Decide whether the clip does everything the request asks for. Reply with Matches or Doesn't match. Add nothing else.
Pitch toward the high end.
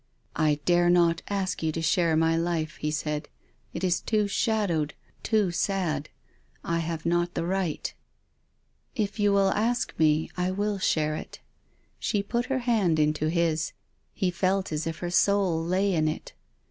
Doesn't match